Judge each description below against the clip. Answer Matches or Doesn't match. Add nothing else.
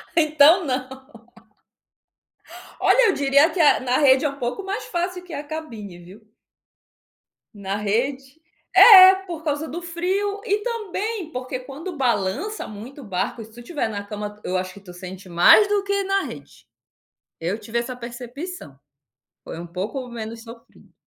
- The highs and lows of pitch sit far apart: Matches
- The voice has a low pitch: Doesn't match